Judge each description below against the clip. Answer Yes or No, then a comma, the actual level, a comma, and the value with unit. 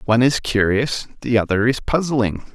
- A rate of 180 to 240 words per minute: No, average, 165 wpm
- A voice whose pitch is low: Yes, low, 120 Hz